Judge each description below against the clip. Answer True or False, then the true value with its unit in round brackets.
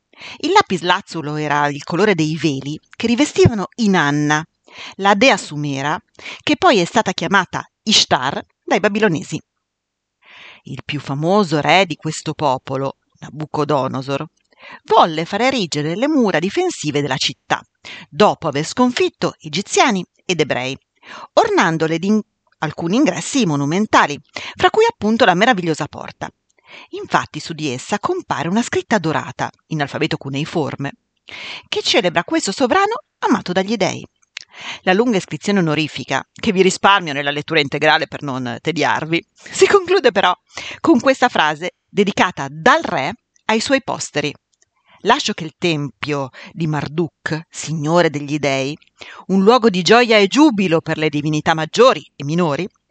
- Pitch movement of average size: False (6.7 semitones)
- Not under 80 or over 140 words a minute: True (135 wpm)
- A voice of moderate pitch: True (170 Hz)